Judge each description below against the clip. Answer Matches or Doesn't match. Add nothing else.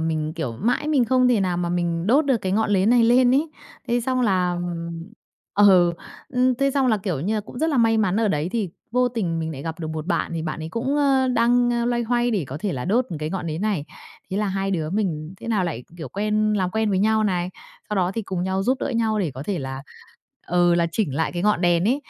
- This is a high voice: Matches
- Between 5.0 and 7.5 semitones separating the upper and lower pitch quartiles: Matches